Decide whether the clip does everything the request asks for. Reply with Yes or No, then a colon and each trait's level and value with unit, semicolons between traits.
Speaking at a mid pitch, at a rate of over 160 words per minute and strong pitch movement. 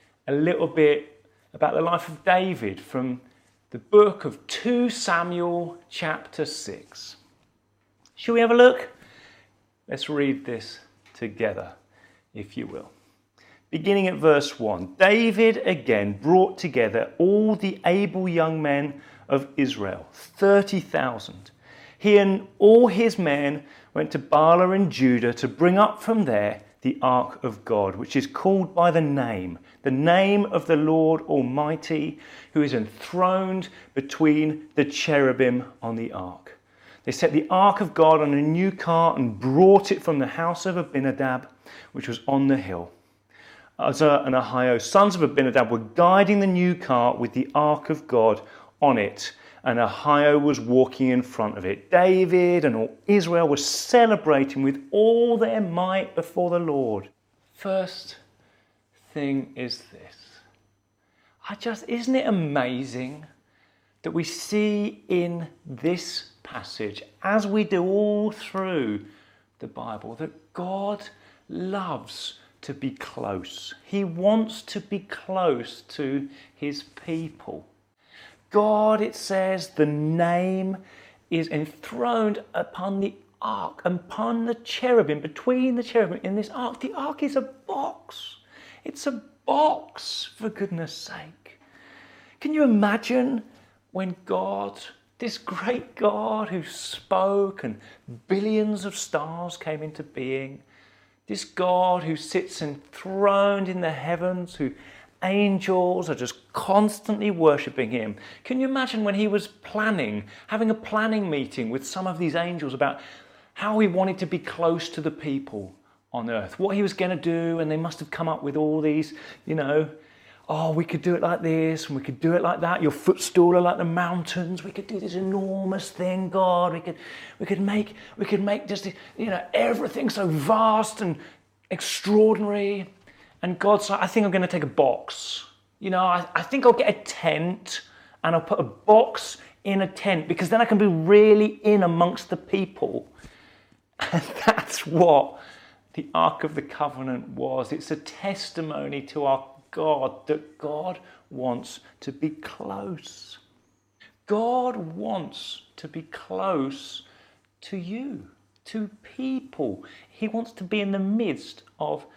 No: medium, 170 Hz; average, 150 wpm; wide, 6.3 semitones